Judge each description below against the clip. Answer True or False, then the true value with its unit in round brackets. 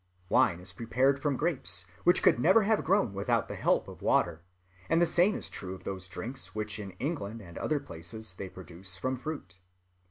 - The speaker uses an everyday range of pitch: False (8.2 semitones)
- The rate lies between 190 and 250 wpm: True (195 wpm)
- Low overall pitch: True (110 Hz)